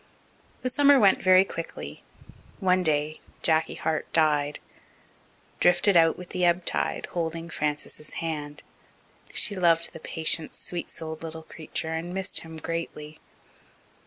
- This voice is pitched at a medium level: Yes, medium, 165 Hz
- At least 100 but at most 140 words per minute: Yes, slow, 135 wpm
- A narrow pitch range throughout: Yes, narrow, 2.2 semitones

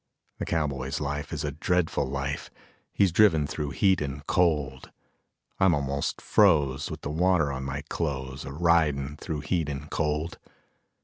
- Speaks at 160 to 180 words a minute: No, average, 150 wpm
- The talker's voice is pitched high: No, very low, 75 Hz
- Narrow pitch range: No, average, 3.1 semitones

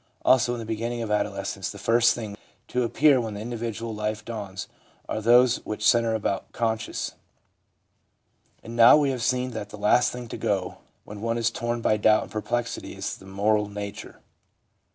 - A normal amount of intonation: No, narrow, 2.1 semitones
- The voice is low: Yes, low, 115 Hz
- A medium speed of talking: Yes, average, 185 wpm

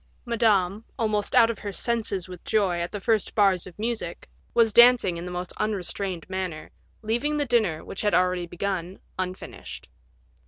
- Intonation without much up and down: No, average, 3.8 semitones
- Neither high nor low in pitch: No, high, 200 Hz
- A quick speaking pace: No, average, 170 wpm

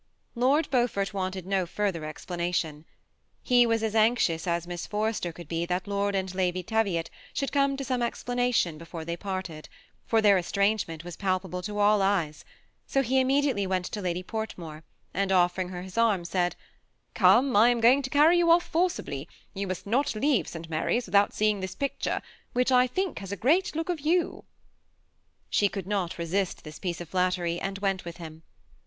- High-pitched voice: Yes, high, 195 Hz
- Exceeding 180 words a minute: Yes, average, 190 wpm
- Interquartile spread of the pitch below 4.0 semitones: No, wide, 5.4 semitones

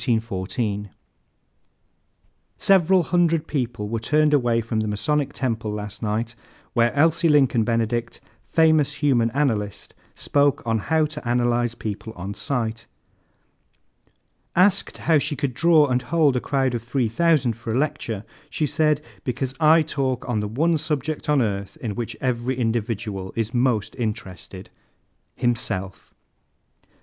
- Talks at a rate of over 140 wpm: No, slow, 135 wpm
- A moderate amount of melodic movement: Yes, average, 4.9 semitones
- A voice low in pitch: Yes, low, 120 Hz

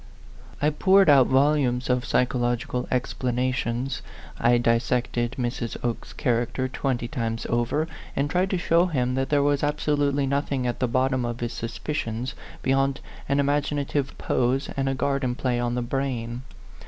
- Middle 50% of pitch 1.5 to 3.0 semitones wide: Yes, average, 2.7 semitones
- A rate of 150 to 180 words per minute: Yes, average, 155 wpm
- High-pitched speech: No, low, 130 Hz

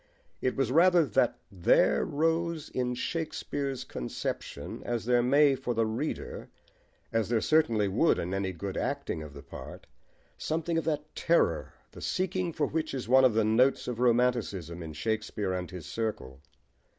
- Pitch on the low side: Yes, low, 125 Hz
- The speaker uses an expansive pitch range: Yes, wide, 7.0 semitones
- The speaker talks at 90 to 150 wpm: No, average, 165 wpm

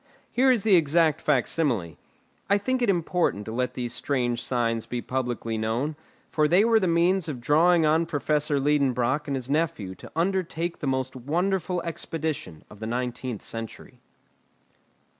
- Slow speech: No, average, 160 wpm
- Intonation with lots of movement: Yes, wide, 5.7 semitones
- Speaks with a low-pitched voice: No, medium, 150 Hz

